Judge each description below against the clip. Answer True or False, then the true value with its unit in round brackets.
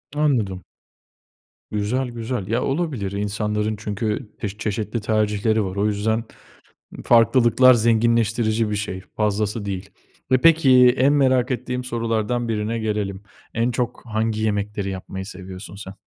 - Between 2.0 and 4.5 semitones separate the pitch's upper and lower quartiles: True (2.6 semitones)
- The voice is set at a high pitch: False (110 Hz)